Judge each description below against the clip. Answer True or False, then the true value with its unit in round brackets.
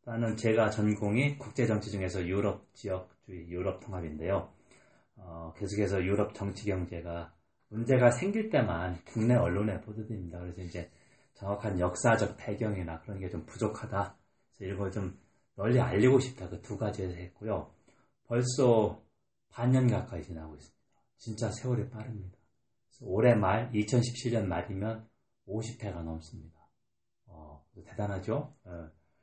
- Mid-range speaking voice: False (105 Hz)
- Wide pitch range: False (4.1 semitones)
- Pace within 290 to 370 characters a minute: True (300 characters per minute)